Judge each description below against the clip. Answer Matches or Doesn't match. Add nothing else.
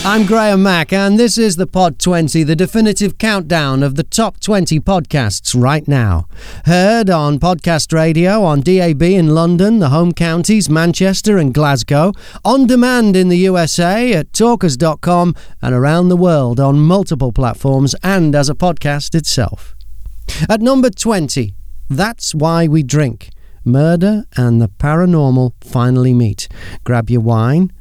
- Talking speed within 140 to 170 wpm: Matches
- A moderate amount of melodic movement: Doesn't match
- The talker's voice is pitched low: Doesn't match